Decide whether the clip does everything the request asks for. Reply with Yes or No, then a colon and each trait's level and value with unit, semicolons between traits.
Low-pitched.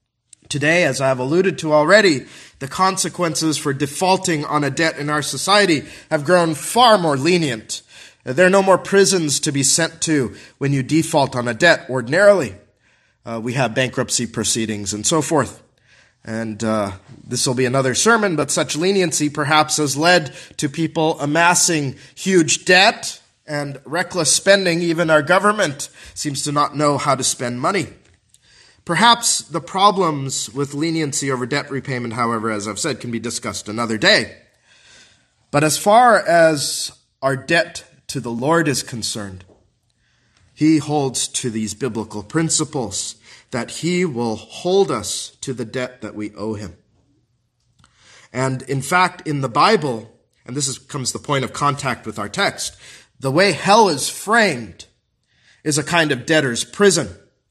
No: medium, 145 Hz